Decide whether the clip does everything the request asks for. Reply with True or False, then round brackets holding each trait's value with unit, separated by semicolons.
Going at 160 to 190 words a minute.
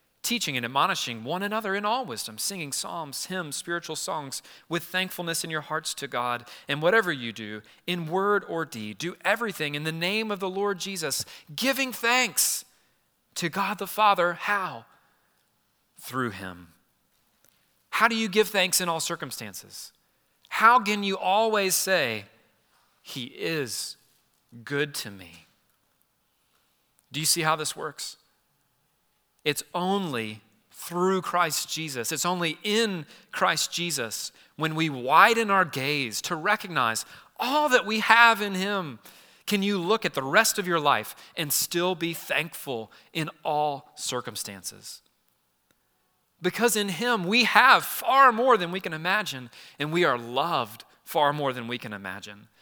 False (150 wpm)